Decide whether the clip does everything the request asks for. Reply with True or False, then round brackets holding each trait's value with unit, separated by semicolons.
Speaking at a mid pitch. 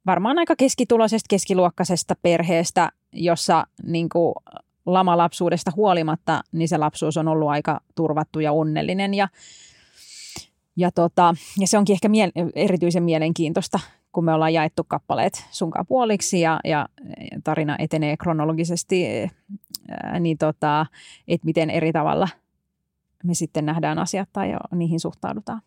True (170 Hz)